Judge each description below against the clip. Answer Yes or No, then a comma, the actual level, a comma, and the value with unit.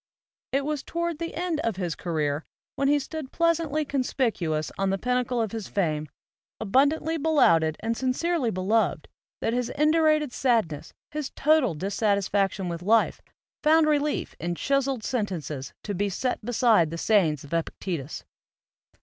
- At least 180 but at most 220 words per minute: No, average, 155 wpm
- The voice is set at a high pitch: Yes, high, 230 Hz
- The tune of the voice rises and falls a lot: Yes, wide, 8.4 semitones